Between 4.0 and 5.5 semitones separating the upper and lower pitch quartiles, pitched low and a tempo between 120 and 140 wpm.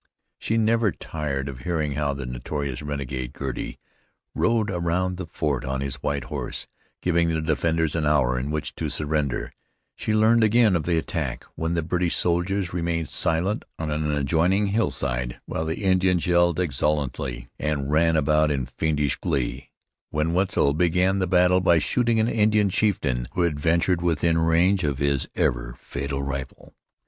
No: average, 4.3 semitones; very low, 80 Hz; average, 165 wpm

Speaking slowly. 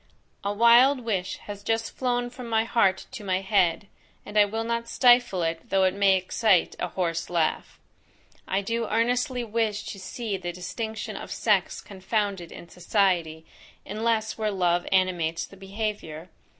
No: average, 160 wpm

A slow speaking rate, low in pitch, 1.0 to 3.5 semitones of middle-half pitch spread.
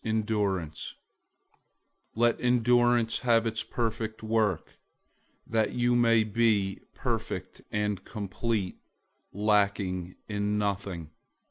Yes: slow, 90 wpm; low, 110 Hz; narrow, 2.4 semitones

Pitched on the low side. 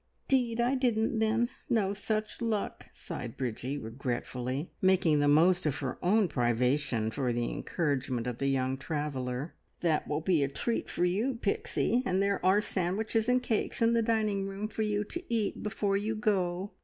No: medium, 185 Hz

